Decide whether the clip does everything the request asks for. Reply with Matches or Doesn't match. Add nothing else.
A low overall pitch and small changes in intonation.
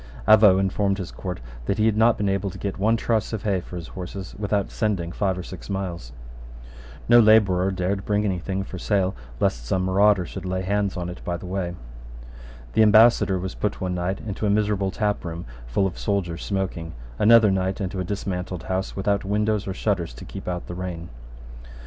Matches